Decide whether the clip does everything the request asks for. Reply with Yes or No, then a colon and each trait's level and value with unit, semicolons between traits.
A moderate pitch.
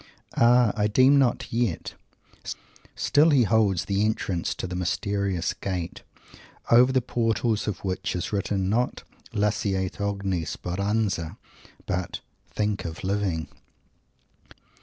No: low, 100 Hz